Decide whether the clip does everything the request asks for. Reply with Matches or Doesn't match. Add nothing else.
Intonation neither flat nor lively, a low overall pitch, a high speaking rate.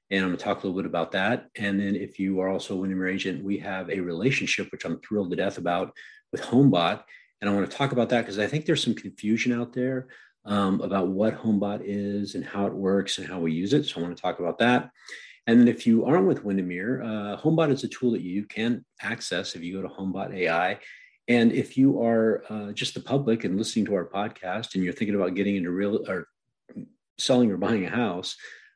Matches